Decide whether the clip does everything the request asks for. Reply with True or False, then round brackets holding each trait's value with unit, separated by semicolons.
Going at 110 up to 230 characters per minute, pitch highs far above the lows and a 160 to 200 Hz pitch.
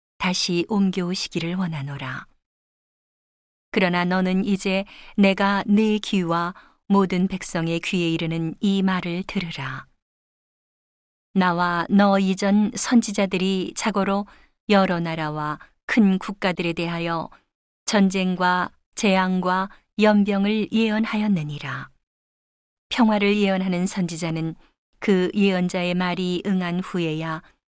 False (225 characters per minute; 2.7 semitones; 185 Hz)